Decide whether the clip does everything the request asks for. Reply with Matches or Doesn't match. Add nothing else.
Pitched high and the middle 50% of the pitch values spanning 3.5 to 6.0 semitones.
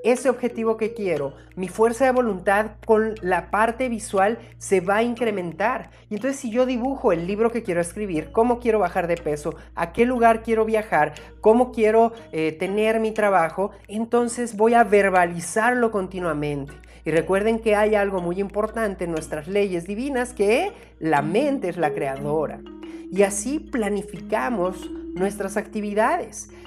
Matches